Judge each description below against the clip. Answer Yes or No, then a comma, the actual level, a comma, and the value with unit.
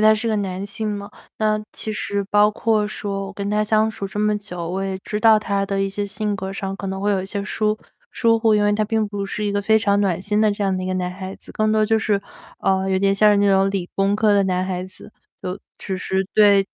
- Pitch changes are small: Yes, narrow, 1.6 semitones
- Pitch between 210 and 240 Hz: No, high, 200 Hz